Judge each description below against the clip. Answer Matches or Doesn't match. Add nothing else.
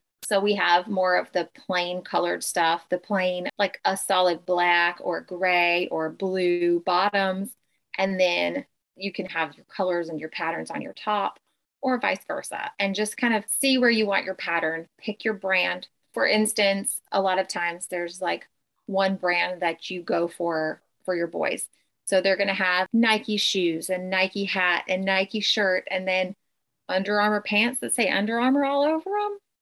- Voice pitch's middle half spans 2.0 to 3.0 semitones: Matches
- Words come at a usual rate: Matches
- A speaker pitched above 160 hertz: Matches